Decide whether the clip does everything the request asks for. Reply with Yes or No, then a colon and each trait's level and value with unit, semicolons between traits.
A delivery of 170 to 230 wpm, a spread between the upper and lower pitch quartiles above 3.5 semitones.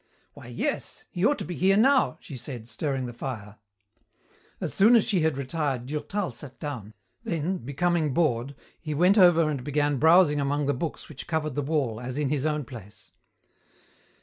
Yes: average, 180 wpm; average, 4.5 semitones